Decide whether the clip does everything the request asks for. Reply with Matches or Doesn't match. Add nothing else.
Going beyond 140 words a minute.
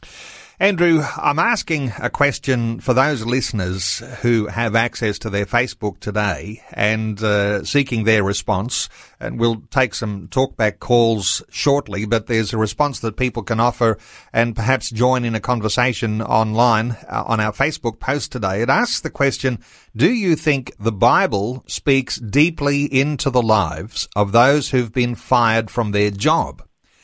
Matches